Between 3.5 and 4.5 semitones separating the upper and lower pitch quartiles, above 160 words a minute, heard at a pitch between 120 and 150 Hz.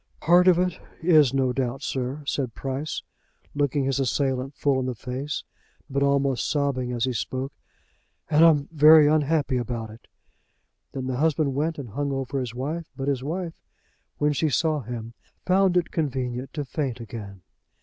No: average, 3.1 semitones; average, 170 wpm; low, 135 Hz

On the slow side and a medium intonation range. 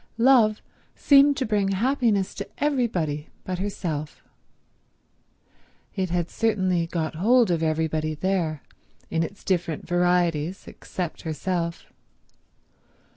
Yes: slow, 105 wpm; average, 4.6 semitones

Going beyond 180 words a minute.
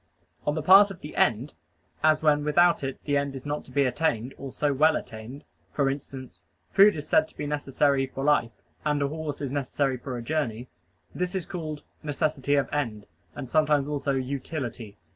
Yes: average, 195 wpm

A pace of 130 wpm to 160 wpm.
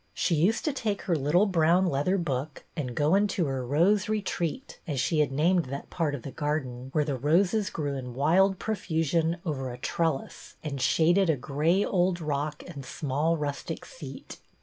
No: average, 180 wpm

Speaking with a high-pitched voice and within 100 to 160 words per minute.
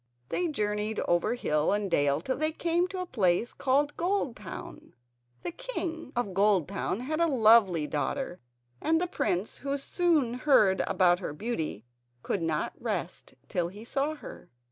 Yes: high, 230 Hz; average, 155 wpm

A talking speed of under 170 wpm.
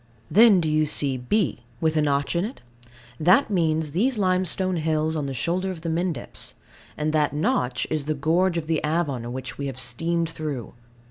No: average, 190 wpm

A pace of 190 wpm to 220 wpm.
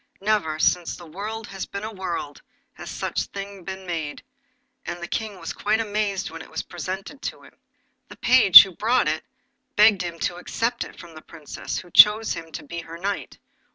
Yes: average, 200 wpm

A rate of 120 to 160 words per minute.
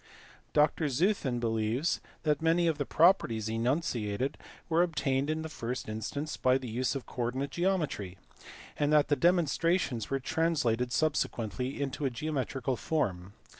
Yes: average, 140 wpm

